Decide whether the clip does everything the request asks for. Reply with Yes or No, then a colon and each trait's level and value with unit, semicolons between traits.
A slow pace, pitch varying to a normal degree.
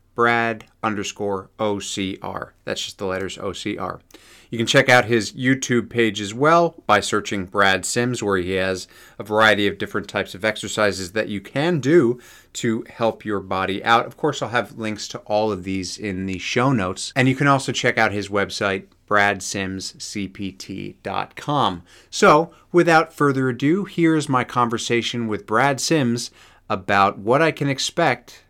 No: average, 160 wpm; average, 4.1 semitones